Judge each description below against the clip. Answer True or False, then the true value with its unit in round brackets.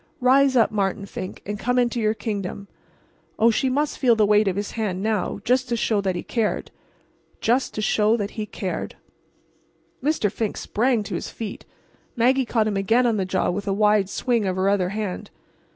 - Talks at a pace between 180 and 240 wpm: True (185 wpm)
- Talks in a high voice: True (215 Hz)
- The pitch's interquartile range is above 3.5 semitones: False (3.1 semitones)